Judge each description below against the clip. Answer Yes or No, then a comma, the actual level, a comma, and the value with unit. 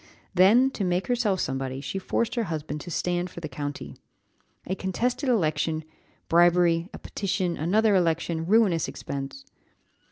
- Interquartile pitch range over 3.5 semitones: Yes, average, 4.2 semitones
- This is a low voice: No, medium, 175 Hz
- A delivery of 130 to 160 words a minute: Yes, average, 140 wpm